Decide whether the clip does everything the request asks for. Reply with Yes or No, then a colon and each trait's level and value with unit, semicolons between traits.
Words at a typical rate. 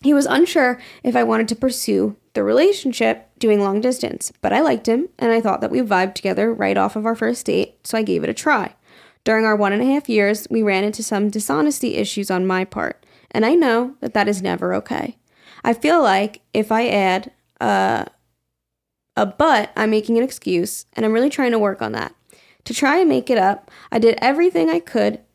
No: fast, 220 wpm